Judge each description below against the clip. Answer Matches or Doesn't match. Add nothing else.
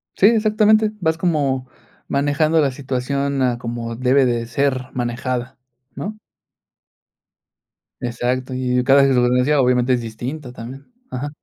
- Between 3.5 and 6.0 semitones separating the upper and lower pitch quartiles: Doesn't match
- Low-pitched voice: Matches